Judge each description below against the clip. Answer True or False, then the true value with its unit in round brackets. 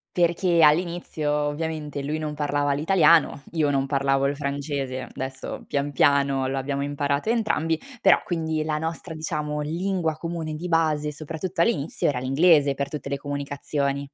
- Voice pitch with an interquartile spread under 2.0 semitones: False (2.4 semitones)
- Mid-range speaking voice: True (150 Hz)